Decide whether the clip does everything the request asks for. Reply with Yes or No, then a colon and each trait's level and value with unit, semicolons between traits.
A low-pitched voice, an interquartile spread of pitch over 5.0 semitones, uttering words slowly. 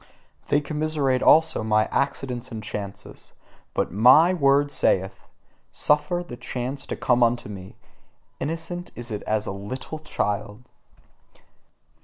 Yes: low, 130 Hz; wide, 5.6 semitones; slow, 125 wpm